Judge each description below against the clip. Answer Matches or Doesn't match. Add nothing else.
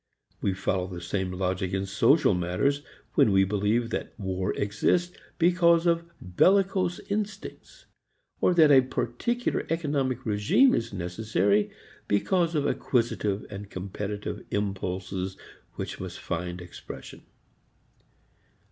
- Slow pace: Matches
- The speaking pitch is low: Matches